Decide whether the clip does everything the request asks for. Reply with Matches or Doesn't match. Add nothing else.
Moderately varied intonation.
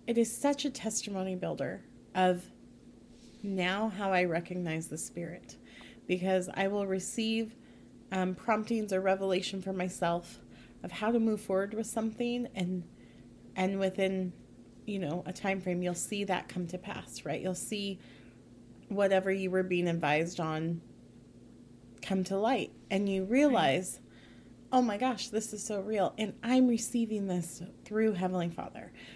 Matches